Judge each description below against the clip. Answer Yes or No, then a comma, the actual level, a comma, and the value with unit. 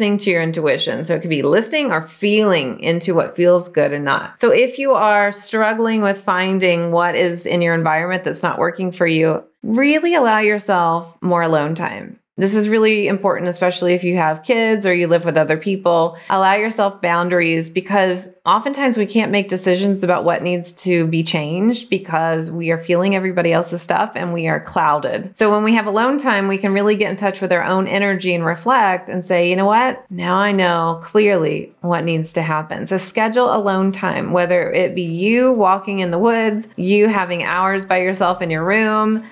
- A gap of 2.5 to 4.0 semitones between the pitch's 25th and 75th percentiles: Yes, average, 3.4 semitones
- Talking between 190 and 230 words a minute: Yes, average, 200 wpm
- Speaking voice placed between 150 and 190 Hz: Yes, medium, 185 Hz